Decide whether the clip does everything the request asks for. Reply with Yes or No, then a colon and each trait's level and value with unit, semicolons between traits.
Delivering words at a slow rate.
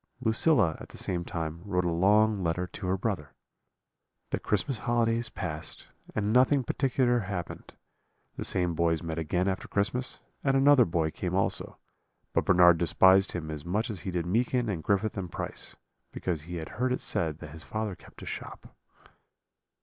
No: average, 175 wpm